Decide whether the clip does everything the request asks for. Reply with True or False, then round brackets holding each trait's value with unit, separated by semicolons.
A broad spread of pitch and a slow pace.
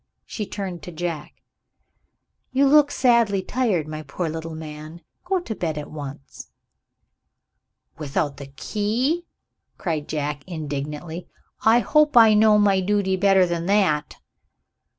True (5.8 semitones; 130 wpm)